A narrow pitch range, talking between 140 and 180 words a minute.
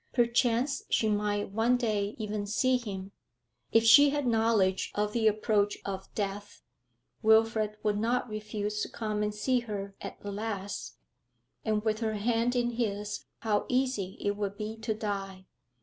Yes: narrow, 1.9 semitones; average, 160 wpm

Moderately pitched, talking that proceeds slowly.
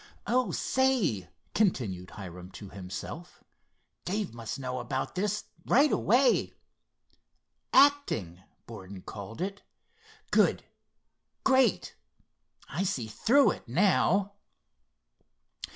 Yes: medium, 175 Hz; slow, 90 wpm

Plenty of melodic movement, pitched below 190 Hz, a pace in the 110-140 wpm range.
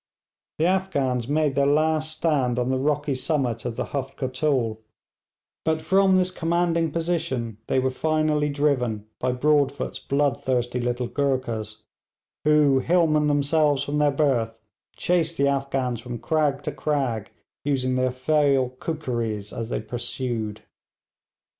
No: average, 3.7 semitones; medium, 140 Hz; slow, 135 wpm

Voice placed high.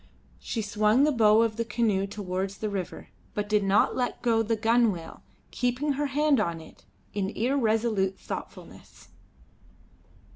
Yes: high, 220 Hz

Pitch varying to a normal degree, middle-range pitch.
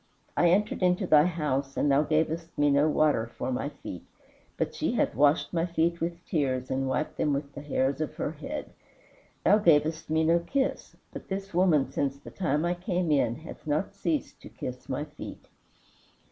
Yes: average, 3.6 semitones; medium, 155 Hz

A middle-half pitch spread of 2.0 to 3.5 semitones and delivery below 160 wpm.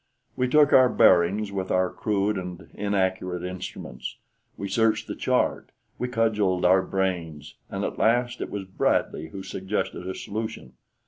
Yes: average, 2.9 semitones; average, 150 wpm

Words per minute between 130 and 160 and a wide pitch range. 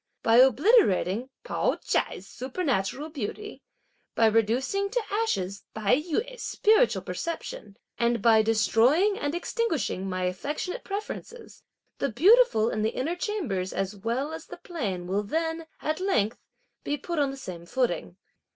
Yes: average, 140 wpm; wide, 8.9 semitones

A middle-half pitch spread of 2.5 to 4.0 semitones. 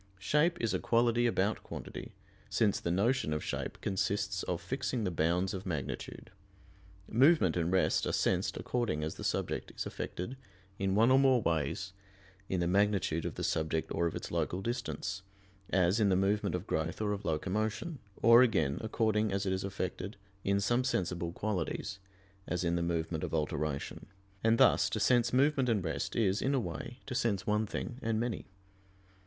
No: average, 4.9 semitones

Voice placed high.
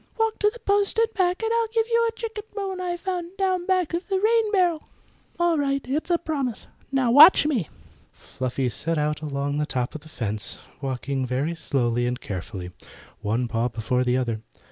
Yes: very high, 275 Hz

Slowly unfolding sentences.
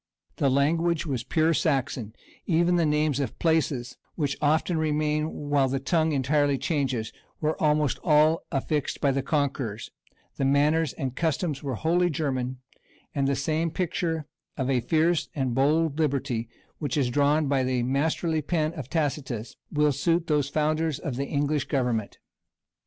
No: average, 155 wpm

